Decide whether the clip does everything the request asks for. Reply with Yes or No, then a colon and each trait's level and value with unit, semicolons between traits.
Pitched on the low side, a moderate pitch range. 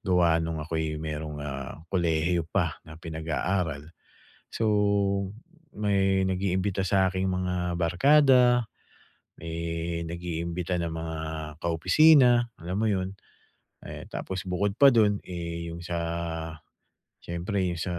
Yes: very low, 90 Hz; average, 3.1 semitones